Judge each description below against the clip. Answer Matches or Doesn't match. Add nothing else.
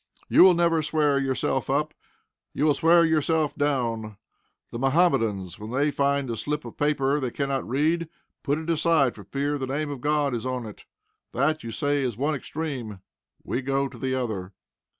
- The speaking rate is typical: Matches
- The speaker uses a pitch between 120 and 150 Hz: Matches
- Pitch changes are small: Doesn't match